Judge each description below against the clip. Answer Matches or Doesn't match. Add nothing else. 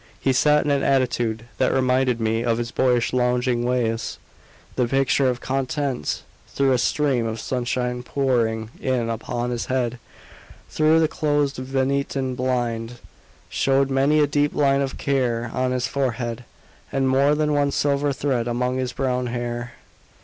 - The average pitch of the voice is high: Doesn't match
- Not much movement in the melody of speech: Matches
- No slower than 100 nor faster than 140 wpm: Doesn't match